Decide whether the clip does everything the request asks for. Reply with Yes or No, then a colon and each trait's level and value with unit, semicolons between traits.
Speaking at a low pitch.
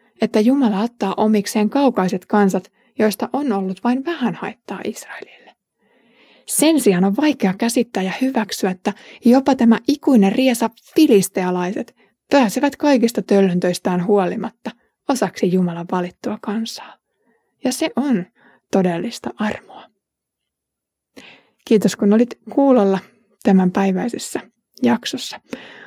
No: high, 220 Hz